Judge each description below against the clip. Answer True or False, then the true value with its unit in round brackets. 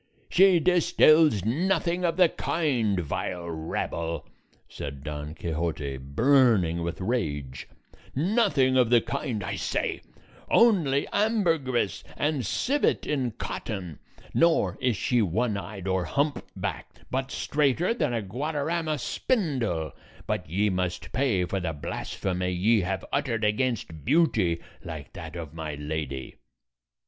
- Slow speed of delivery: True (125 wpm)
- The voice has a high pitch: False (110 Hz)